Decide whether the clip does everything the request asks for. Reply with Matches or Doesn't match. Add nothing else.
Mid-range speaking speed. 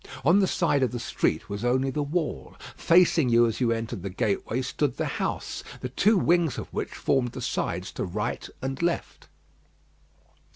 Matches